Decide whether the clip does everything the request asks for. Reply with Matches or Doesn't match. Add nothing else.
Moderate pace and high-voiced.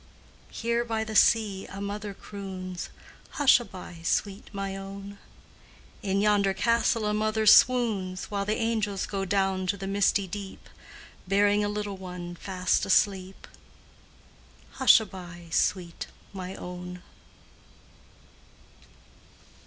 Doesn't match